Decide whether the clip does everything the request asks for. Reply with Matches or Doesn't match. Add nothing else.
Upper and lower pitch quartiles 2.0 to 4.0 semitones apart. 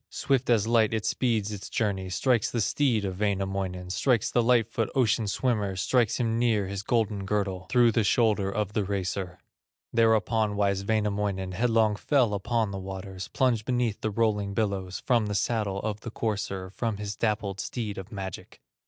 Matches